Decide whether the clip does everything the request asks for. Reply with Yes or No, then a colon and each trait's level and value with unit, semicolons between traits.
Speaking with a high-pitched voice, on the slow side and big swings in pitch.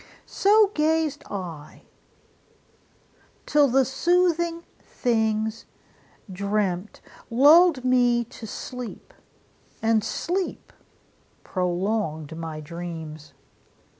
Yes: high, 225 Hz; slow, 75 wpm; wide, 8.7 semitones